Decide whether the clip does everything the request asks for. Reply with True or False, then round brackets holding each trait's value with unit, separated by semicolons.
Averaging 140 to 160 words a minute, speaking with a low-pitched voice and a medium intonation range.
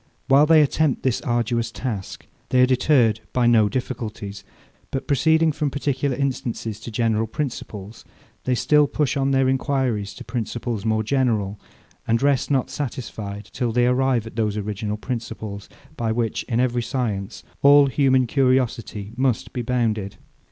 True (150 wpm; 120 Hz; 3.4 semitones)